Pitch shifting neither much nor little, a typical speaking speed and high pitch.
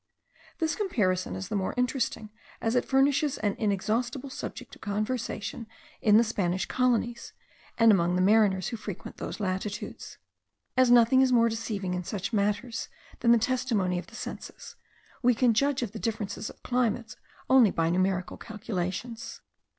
Yes: average, 3.8 semitones; average, 160 wpm; high, 225 Hz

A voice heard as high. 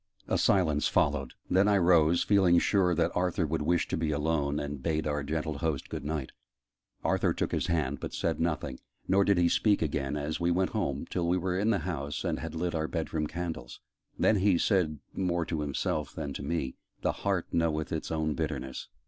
No: very low, 80 Hz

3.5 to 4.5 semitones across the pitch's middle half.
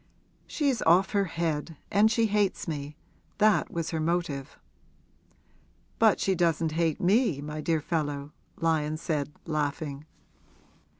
Yes: average, 4.1 semitones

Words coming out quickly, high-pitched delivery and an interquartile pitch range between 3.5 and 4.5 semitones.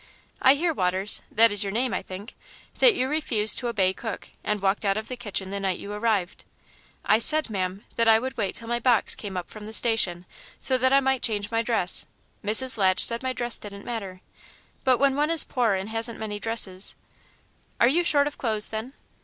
Yes: fast, 220 wpm; high, 225 Hz; average, 4.1 semitones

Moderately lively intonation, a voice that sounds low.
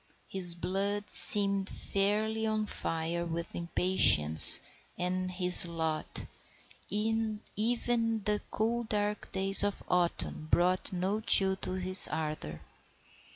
No: average, 3.3 semitones; high, 190 Hz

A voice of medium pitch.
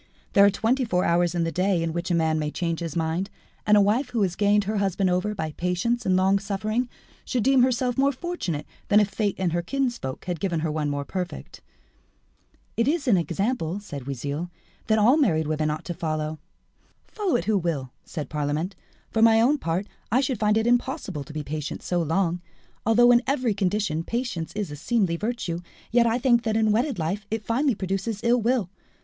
No: high, 195 Hz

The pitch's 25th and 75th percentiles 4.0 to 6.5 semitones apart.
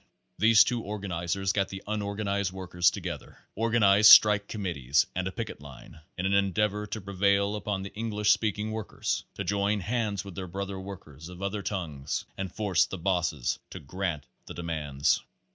No: average, 2.7 semitones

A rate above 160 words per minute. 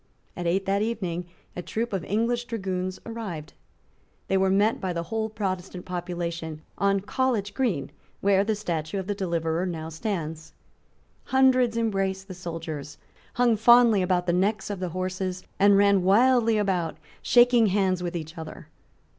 No: average, 155 wpm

